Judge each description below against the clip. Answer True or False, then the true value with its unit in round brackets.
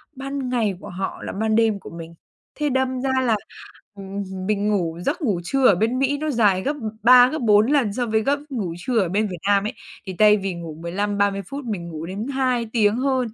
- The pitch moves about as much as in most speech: True (4.7 semitones)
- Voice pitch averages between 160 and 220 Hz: True (215 Hz)